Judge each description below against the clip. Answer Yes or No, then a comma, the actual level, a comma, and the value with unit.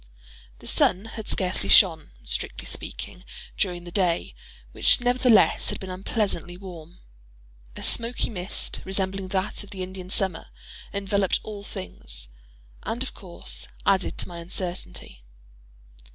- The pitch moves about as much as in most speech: No, narrow, 2.3 semitones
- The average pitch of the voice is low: No, high, 190 Hz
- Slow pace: Yes, slow, 125 wpm